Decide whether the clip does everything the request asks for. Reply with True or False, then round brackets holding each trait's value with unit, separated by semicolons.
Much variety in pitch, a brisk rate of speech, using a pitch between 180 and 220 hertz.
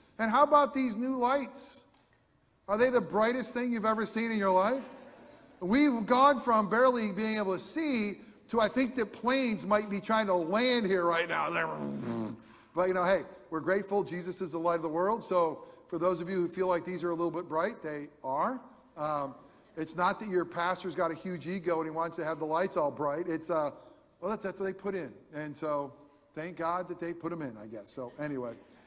True (5.8 semitones; 225 wpm; 185 Hz)